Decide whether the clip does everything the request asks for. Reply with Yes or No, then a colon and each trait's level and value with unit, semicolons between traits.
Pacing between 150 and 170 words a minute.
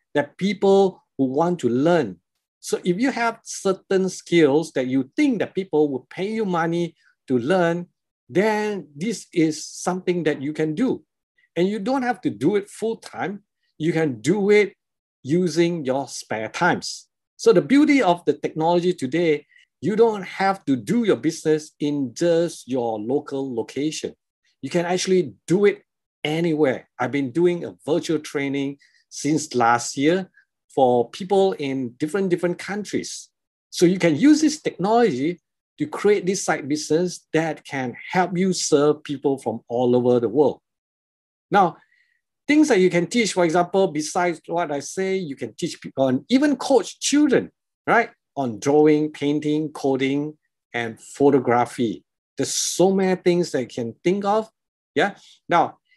Yes: average, 160 wpm